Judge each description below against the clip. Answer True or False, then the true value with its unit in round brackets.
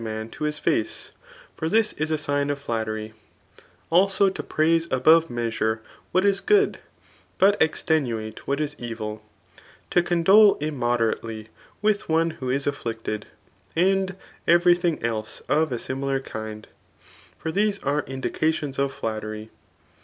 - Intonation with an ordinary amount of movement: False (6.8 semitones)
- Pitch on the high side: False (145 Hz)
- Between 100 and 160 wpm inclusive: True (140 wpm)